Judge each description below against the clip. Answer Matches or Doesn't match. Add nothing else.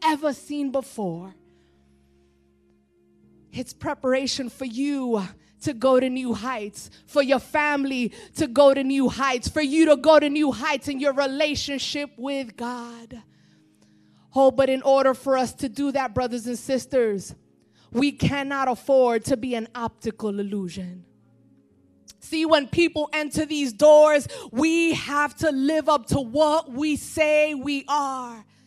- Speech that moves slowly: Doesn't match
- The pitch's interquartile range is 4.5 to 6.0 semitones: Doesn't match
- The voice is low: Doesn't match